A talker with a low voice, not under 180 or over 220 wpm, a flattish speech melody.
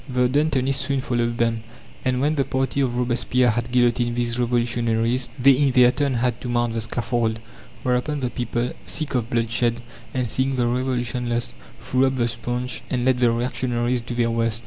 Yes: low, 125 Hz; average, 190 wpm; narrow, 1.4 semitones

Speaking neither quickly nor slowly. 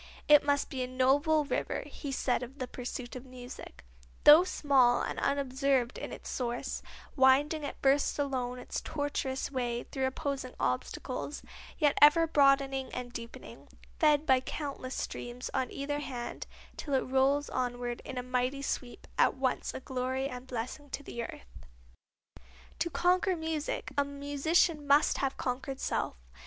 Yes: average, 160 wpm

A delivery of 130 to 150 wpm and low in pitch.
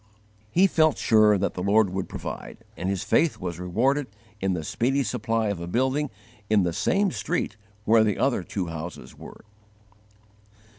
No: average, 165 wpm; low, 110 Hz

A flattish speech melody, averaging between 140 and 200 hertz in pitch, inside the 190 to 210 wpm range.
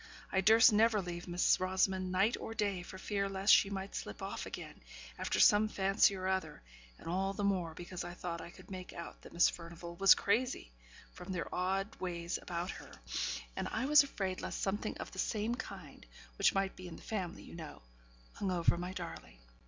Yes: narrow, 2.2 semitones; high, 190 Hz; average, 200 wpm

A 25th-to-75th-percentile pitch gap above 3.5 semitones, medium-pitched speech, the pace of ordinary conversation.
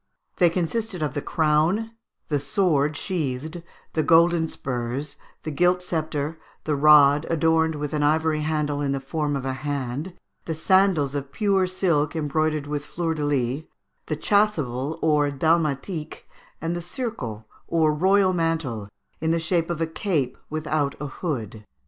No: average, 2.7 semitones; medium, 155 Hz; average, 155 wpm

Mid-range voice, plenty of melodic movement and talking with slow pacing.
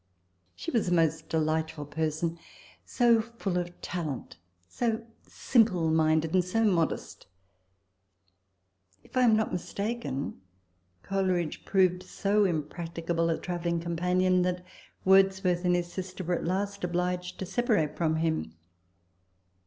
No: medium, 180 Hz; average, 2.9 semitones; slow, 125 wpm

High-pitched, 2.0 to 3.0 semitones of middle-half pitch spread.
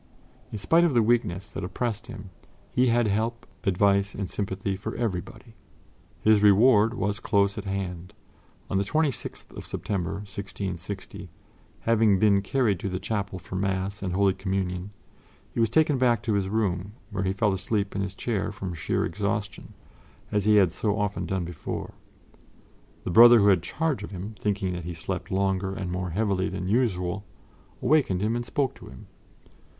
No: low, 100 Hz; average, 2.7 semitones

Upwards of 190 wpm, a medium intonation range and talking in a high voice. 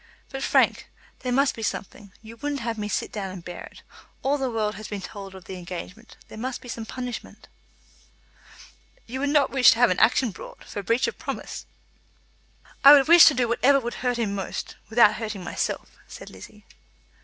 Yes: average, 200 wpm; average, 4.0 semitones; high, 230 Hz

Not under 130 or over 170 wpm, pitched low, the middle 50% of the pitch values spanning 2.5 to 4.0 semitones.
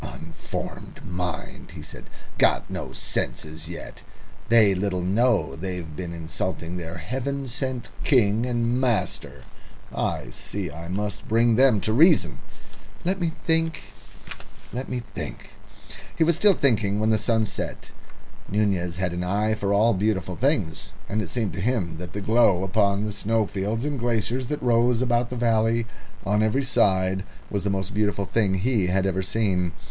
No: average, 160 wpm; low, 105 Hz; average, 4.4 semitones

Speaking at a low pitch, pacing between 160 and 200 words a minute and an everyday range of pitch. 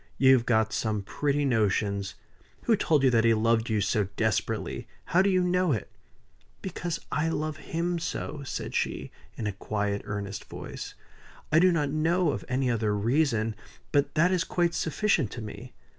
No: low, 130 Hz; average, 175 wpm; wide, 7.1 semitones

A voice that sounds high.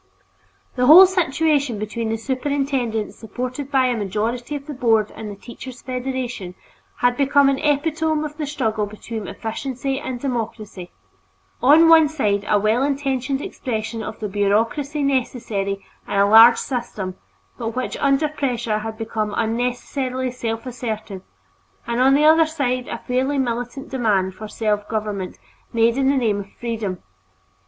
Yes: high, 245 Hz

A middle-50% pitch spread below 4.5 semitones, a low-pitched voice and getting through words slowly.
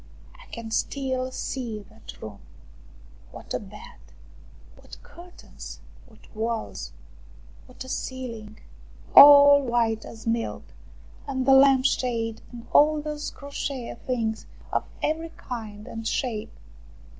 No: average, 3.6 semitones; very high, 250 Hz; slow, 120 wpm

